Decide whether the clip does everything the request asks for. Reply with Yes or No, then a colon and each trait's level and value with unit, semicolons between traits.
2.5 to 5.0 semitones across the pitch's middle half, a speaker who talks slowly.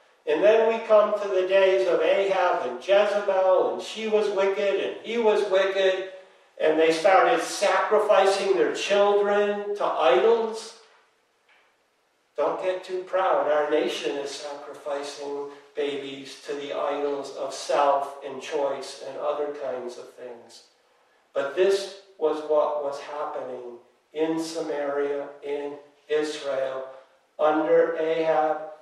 No: wide, 5.5 semitones; slow, 125 wpm